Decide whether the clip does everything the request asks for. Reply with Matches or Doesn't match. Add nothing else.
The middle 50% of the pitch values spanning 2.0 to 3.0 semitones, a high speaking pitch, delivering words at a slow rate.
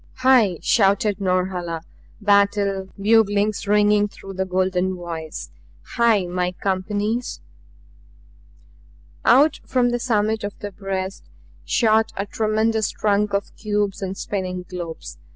Matches